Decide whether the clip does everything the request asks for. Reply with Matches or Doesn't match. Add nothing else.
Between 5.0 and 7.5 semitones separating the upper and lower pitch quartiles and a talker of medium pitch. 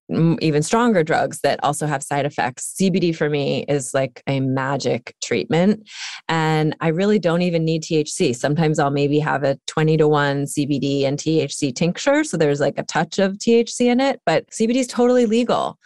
Matches